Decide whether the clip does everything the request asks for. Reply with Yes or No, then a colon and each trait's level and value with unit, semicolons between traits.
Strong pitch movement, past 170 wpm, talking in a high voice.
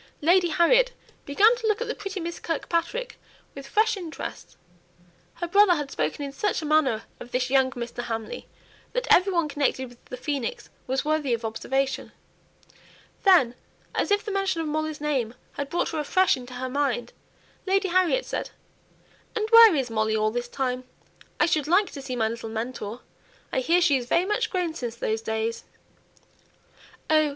Yes: wide, 6.9 semitones; average, 180 wpm; very high, 295 Hz